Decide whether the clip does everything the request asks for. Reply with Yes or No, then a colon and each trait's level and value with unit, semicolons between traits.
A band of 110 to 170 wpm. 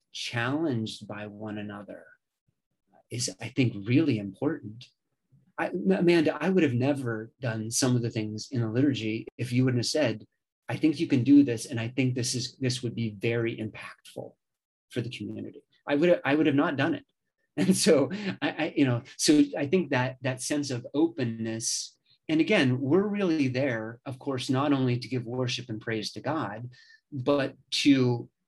No: average, 190 wpm